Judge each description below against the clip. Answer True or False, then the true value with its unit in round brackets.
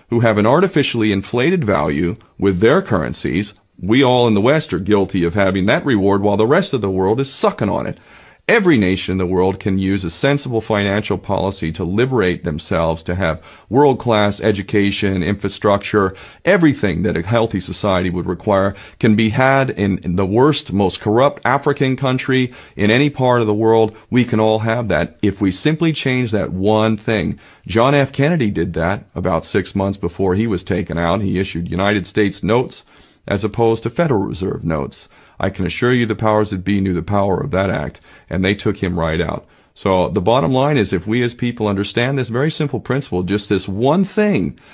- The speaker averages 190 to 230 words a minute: True (195 wpm)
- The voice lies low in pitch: True (105 Hz)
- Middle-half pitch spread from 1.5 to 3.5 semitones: False (4.2 semitones)